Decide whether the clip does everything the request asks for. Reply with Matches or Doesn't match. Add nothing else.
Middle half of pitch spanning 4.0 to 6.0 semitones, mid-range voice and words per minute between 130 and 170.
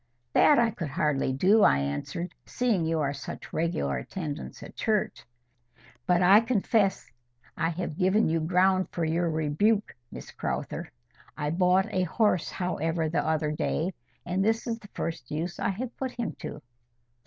Matches